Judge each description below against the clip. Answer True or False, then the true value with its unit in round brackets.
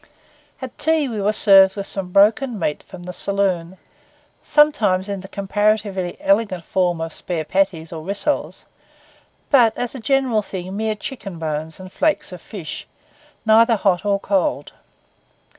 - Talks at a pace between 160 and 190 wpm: False (150 wpm)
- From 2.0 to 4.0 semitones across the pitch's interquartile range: True (3.5 semitones)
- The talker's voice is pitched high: True (200 Hz)